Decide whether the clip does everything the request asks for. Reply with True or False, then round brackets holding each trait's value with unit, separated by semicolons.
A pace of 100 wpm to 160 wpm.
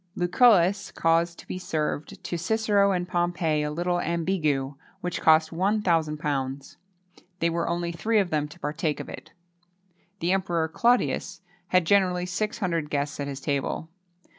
True (150 wpm)